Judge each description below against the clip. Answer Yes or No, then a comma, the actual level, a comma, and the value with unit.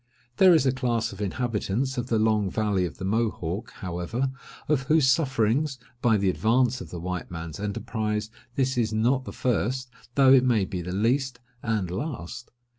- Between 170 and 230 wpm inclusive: Yes, average, 180 wpm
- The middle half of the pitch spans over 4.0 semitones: Yes, average, 4.7 semitones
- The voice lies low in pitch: Yes, low, 115 Hz